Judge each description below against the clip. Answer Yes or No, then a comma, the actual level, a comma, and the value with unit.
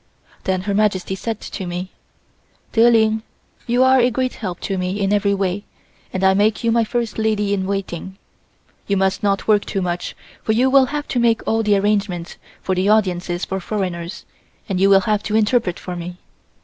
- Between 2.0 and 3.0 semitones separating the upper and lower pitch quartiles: Yes, average, 2.7 semitones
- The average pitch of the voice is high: Yes, high, 200 Hz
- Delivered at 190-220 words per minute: Yes, average, 200 wpm